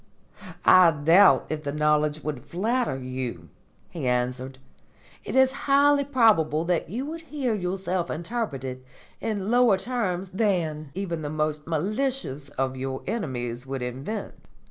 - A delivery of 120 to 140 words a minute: Yes, slow, 135 wpm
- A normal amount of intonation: No, wide, 8.2 semitones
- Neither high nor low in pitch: Yes, medium, 165 Hz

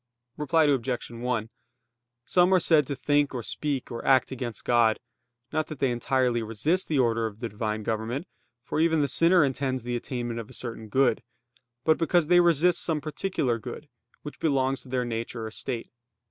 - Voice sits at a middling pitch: No, low, 130 Hz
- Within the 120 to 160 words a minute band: No, average, 185 wpm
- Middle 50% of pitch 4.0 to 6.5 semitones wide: Yes, average, 4.4 semitones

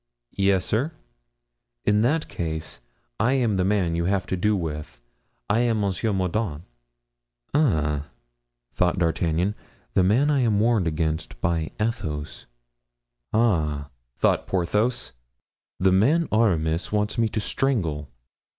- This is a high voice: No, very low, 95 Hz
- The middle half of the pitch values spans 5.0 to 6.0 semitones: Yes, wide, 5.5 semitones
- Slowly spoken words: Yes, slow, 125 wpm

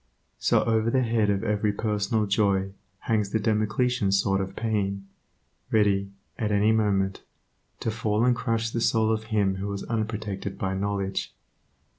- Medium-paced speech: Yes, average, 155 wpm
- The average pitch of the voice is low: Yes, low, 105 Hz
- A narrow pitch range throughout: Yes, narrow, 2.1 semitones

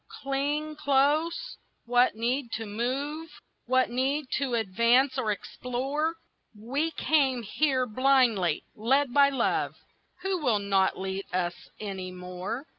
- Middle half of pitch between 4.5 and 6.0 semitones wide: Yes, average, 4.9 semitones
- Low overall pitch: No, very high, 255 Hz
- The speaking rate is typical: No, slow, 120 wpm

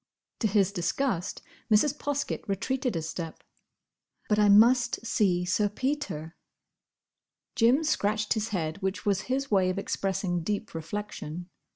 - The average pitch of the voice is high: Yes, high, 205 Hz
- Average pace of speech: No, slow, 130 wpm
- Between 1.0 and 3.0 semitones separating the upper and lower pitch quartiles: No, average, 4.4 semitones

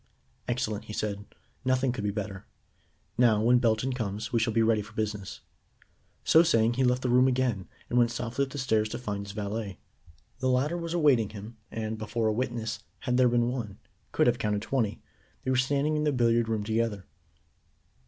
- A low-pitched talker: Yes, low, 115 Hz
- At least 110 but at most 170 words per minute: No, average, 195 wpm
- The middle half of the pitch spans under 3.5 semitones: Yes, average, 3.0 semitones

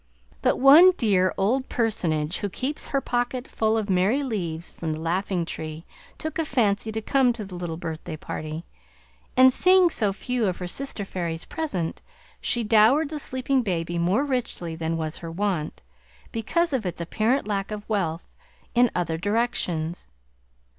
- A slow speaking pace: No, average, 165 wpm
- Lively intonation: Yes, wide, 6.7 semitones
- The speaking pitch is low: No, high, 205 Hz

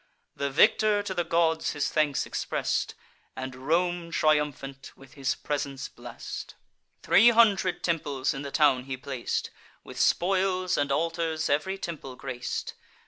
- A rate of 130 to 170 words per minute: Yes, average, 140 wpm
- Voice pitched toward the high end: No, medium, 150 Hz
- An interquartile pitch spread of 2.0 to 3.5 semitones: No, average, 4.3 semitones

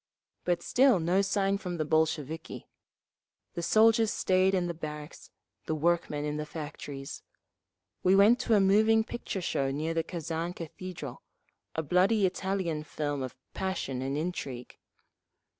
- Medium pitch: Yes, medium, 170 Hz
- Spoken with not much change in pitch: No, average, 4.2 semitones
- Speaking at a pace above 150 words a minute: No, average, 140 wpm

